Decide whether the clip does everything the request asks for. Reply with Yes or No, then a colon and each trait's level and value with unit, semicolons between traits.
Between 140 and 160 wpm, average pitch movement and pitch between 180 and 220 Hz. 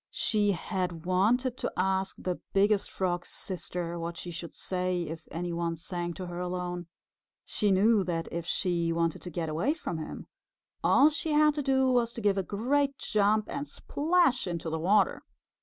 No: average, 180 wpm; average, 4.8 semitones; medium, 185 Hz